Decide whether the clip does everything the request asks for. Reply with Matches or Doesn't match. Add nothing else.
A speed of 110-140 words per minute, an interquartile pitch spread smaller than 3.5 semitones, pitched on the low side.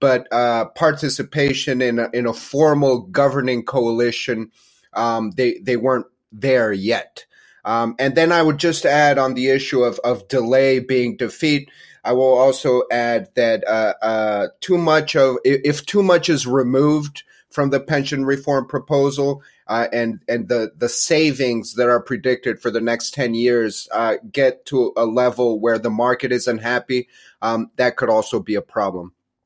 Doesn't match